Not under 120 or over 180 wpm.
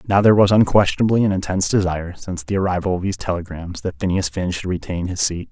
No: average, 195 wpm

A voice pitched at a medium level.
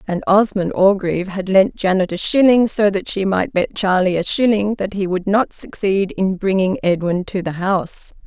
No: high, 195 Hz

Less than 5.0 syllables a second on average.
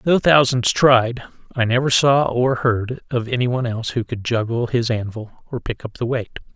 Yes: 4.8 syllables/s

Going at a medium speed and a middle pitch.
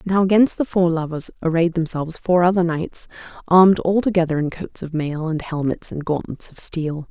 Yes: average, 185 wpm; medium, 170 Hz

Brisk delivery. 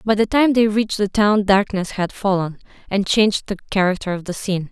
Yes: fast, 215 wpm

